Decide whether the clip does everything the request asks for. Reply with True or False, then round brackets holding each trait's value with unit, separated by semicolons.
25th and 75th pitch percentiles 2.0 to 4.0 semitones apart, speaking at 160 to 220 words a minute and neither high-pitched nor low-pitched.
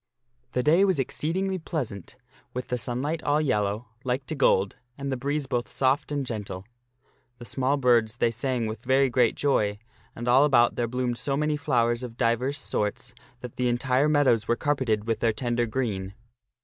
False (3.2 semitones; 180 wpm; 125 Hz)